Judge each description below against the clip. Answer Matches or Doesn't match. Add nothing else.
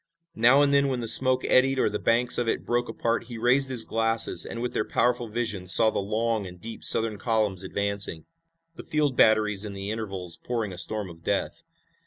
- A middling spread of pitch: Matches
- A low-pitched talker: Matches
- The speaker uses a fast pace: Matches